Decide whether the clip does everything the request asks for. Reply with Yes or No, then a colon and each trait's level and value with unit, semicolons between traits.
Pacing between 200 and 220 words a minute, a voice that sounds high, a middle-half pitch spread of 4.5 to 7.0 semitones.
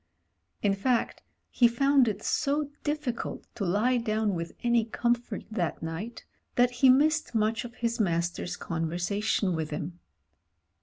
No: average, 140 wpm; high, 225 Hz; average, 5.2 semitones